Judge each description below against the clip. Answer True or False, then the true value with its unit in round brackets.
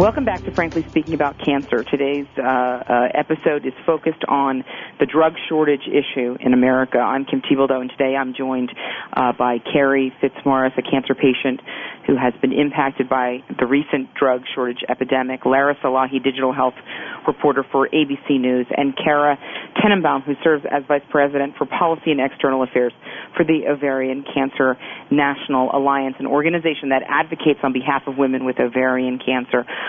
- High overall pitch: False (135 Hz)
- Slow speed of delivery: False (165 wpm)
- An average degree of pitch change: False (2.0 semitones)